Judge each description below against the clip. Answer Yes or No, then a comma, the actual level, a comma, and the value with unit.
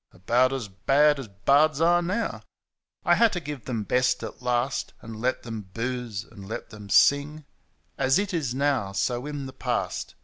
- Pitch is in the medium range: No, low, 130 Hz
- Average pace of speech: Yes, average, 180 wpm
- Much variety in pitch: No, average, 4.6 semitones